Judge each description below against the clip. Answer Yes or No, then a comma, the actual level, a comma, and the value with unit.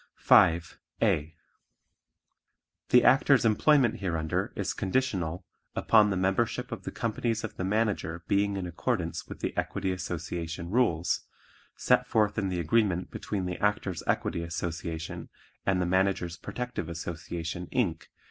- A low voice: Yes, very low, 95 Hz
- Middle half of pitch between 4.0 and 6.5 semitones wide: Yes, average, 4.3 semitones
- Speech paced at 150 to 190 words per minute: No, slow, 135 wpm